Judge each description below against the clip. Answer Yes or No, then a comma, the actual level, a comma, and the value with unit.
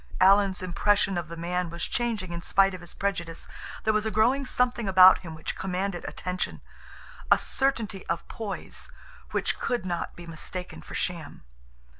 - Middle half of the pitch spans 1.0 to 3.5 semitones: Yes, average, 3.2 semitones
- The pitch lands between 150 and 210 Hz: Yes, medium, 185 Hz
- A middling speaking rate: Yes, average, 165 wpm